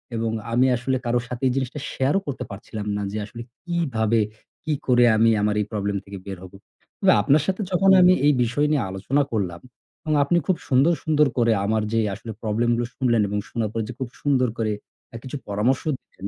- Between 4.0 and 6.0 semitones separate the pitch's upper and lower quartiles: Yes, average, 4.6 semitones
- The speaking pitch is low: Yes, low, 120 Hz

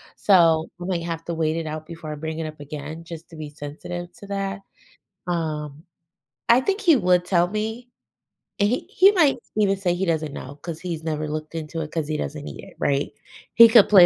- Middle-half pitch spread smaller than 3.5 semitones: No, average, 4.0 semitones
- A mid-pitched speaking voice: Yes, medium, 165 Hz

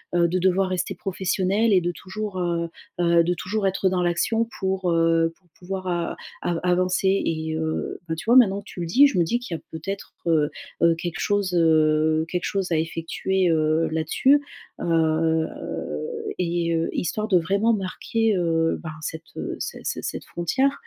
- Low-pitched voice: No, medium, 175 Hz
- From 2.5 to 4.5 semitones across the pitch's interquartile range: Yes, average, 2.8 semitones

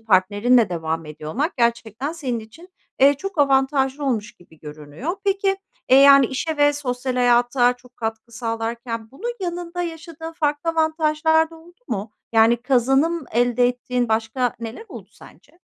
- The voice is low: No, very high, 255 Hz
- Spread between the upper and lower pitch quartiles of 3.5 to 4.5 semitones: No, wide, 5.6 semitones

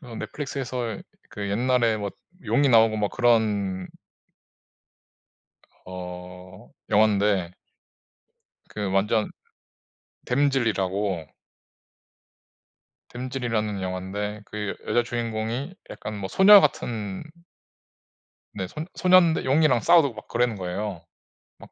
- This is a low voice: Yes, low, 110 Hz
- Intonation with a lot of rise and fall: No, average, 3.9 semitones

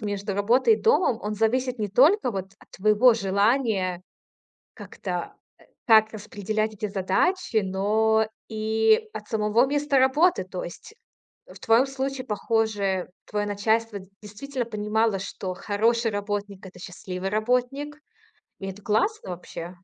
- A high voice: Yes, high, 215 Hz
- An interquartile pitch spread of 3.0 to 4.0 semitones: Yes, average, 3.7 semitones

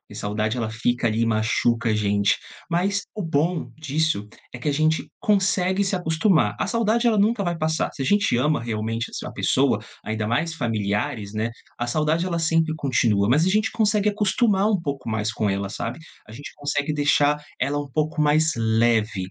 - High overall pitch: No, medium, 145 Hz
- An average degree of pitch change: No, wide, 7.5 semitones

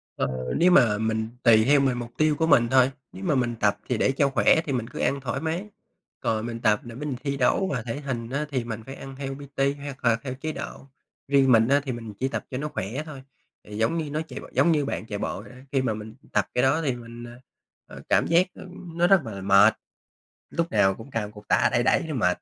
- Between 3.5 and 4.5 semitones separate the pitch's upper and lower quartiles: Yes, average, 4.2 semitones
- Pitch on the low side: Yes, low, 130 Hz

